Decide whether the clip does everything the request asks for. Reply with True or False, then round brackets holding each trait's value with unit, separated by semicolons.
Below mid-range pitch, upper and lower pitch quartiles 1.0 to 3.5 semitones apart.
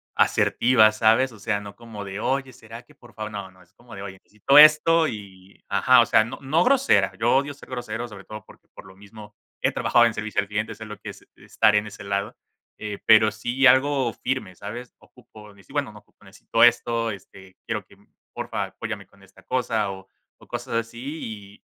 True (110 Hz; 3.1 semitones)